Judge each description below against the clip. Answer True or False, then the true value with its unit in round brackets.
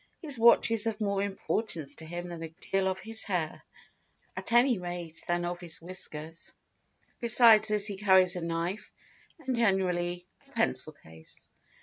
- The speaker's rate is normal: True (165 wpm)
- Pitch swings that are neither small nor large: True (3.8 semitones)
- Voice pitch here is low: False (185 Hz)